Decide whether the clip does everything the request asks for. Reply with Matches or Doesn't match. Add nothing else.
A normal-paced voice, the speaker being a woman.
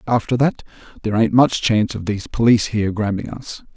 Doesn't match